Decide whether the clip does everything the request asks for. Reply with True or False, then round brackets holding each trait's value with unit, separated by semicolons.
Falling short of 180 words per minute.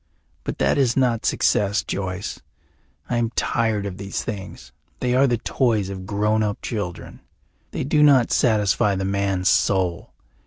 True (155 wpm)